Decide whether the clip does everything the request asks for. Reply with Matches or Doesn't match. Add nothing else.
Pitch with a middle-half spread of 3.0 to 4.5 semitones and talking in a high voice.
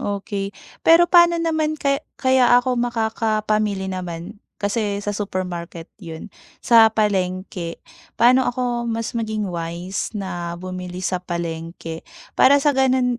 Doesn't match